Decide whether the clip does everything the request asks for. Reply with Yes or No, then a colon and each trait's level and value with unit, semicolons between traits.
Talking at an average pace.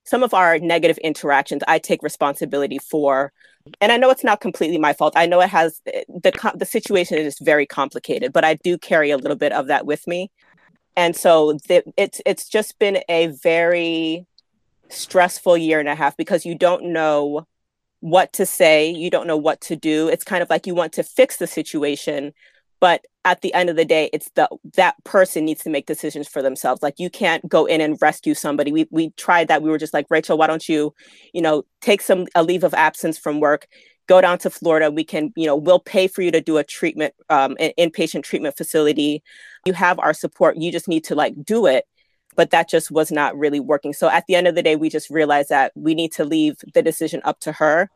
No: fast, 225 wpm